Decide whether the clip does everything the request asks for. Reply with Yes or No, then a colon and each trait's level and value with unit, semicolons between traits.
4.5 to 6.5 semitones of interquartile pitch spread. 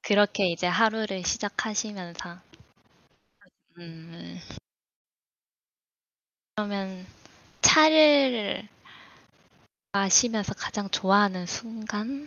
No: average, 3.2 semitones